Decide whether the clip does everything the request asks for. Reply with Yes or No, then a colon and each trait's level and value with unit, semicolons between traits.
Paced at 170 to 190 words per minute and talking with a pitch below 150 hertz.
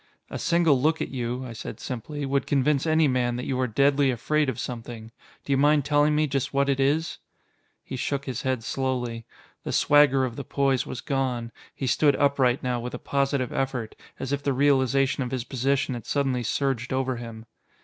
No: average, 200 wpm; low, 135 Hz